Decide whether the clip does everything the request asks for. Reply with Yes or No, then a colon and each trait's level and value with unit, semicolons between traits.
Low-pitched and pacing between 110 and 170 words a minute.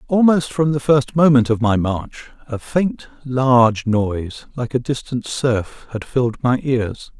Yes: low, 125 Hz; average, 165 wpm